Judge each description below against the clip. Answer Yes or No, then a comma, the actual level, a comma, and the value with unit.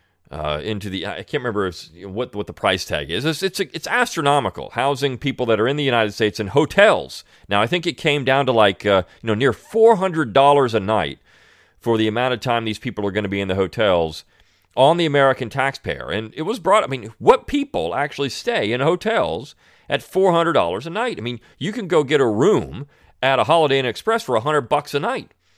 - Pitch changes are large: Yes, wide, 6.7 semitones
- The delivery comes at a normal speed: No, fast, 230 wpm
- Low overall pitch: Yes, low, 130 Hz